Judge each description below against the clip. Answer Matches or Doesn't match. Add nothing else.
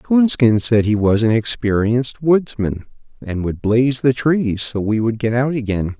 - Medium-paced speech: Matches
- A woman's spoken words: Doesn't match